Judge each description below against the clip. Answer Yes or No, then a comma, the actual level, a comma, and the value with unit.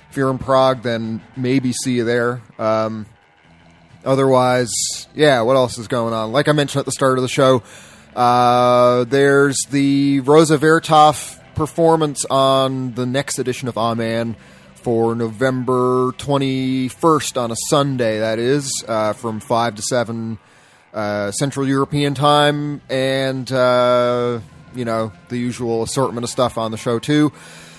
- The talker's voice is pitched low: Yes, low, 125 Hz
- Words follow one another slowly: No, average, 150 wpm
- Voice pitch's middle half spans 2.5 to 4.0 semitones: Yes, average, 3.0 semitones